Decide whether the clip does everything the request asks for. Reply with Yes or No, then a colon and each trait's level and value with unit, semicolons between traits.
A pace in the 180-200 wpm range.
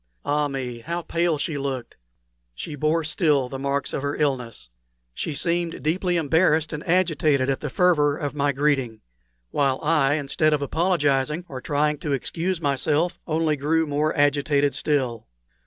No: average, 155 wpm